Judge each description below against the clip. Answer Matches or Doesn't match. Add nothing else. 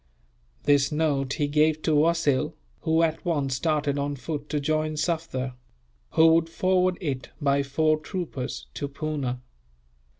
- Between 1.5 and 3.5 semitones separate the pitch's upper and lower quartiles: Matches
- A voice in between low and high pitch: Matches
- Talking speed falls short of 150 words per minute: Matches